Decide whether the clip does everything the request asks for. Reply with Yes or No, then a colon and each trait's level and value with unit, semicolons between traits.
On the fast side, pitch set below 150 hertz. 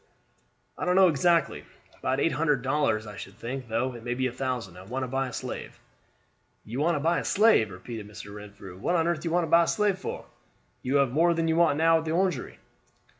Yes: fast, 240 wpm; low, 135 Hz